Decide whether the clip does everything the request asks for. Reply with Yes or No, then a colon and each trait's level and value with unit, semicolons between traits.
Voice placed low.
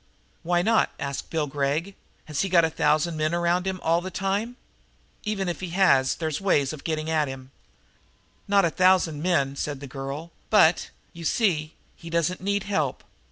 No: medium, 170 Hz